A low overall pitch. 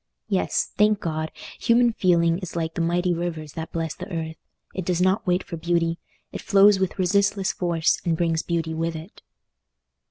No: medium, 170 Hz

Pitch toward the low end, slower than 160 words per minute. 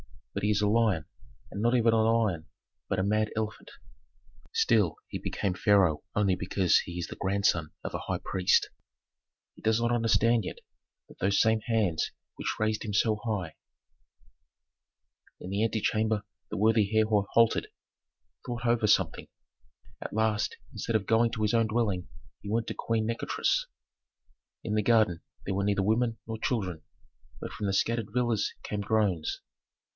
No: low, 110 Hz; average, 165 wpm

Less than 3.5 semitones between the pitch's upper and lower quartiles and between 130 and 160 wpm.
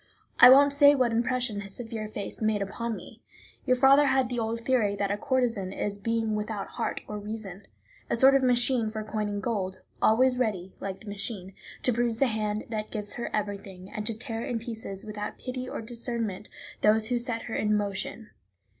No: average, 2.9 semitones; average, 200 wpm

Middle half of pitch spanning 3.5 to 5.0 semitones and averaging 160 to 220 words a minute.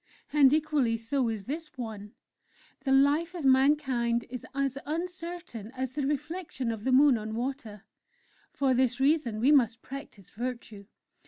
No: average, 4.2 semitones; average, 150 wpm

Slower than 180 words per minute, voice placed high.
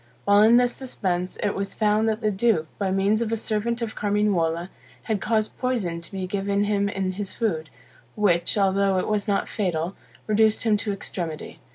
No: average, 190 wpm; high, 205 Hz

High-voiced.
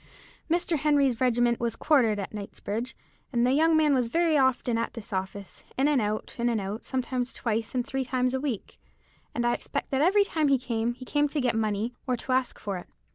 Yes: very high, 250 Hz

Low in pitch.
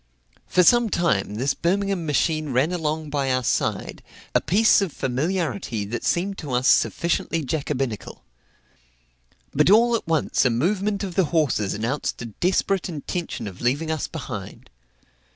No: medium, 155 Hz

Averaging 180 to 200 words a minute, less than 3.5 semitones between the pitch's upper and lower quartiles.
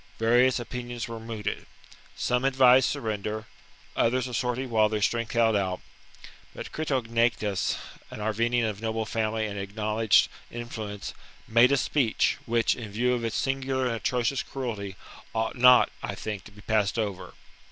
No: average, 155 wpm; narrow, 2.4 semitones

